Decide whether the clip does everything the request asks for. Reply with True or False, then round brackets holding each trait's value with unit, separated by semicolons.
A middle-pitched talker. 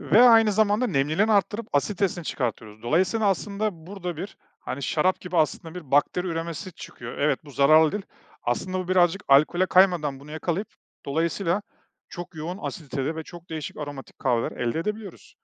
True (170 Hz)